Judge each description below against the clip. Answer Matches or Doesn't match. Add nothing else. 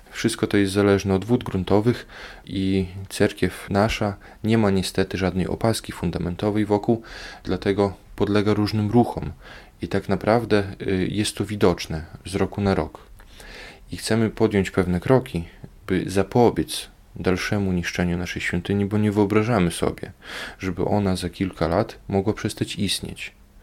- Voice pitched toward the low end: Matches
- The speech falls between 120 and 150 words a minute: Matches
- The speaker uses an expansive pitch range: Doesn't match